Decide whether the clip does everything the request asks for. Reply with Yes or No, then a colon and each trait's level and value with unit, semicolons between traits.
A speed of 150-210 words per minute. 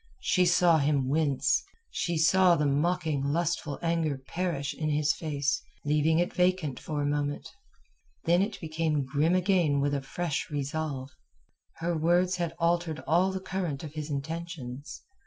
Yes: average, 155 wpm